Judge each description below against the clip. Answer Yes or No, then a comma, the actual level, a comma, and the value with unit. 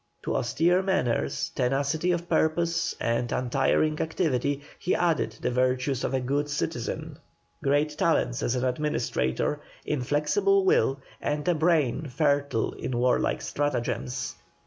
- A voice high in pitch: No, medium, 145 Hz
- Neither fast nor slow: No, slow, 125 wpm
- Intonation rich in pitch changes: No, average, 3.9 semitones